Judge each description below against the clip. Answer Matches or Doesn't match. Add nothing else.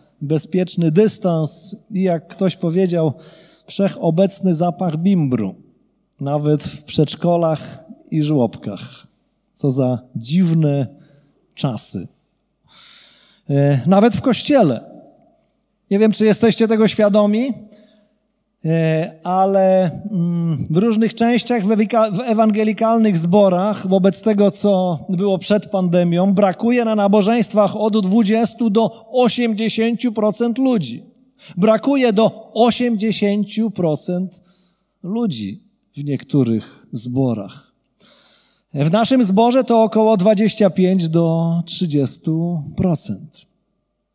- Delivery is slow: Matches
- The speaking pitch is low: Doesn't match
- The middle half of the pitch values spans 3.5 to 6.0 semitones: Matches